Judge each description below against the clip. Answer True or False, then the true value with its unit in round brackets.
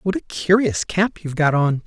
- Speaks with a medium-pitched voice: True (170 Hz)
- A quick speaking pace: True (225 wpm)